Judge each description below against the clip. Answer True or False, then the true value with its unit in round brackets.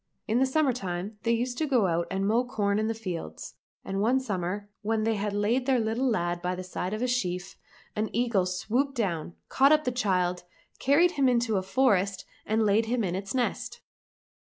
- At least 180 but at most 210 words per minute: True (205 wpm)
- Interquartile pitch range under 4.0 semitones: False (4.8 semitones)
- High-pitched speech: True (215 Hz)